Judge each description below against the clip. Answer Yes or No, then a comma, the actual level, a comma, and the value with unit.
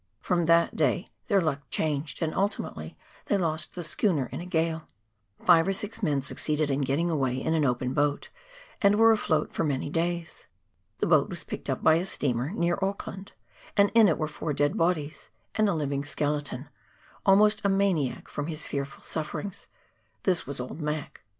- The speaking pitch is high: No, medium, 160 Hz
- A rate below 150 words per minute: No, average, 185 wpm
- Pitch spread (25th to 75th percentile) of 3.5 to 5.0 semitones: Yes, average, 4.4 semitones